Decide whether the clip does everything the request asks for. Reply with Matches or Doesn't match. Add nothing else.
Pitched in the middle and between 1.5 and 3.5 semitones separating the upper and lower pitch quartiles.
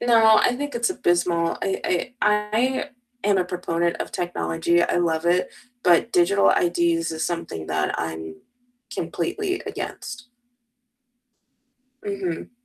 Doesn't match